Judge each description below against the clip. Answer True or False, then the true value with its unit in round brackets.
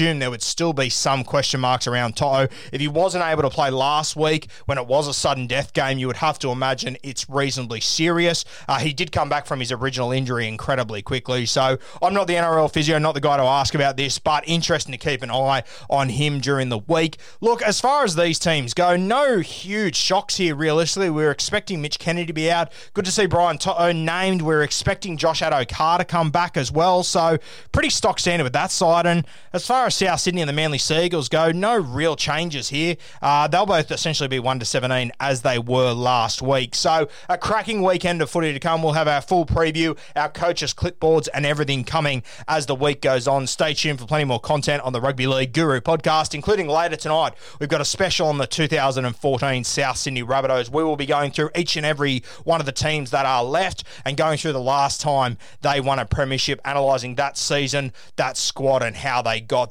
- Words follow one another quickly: True (220 wpm)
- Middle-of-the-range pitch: True (150 Hz)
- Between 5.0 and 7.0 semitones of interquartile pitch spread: False (3.7 semitones)